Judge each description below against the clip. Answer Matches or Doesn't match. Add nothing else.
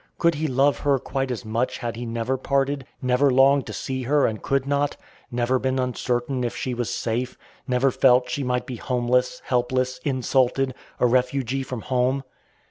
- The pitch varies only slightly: Matches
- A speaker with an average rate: Matches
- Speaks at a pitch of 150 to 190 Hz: Doesn't match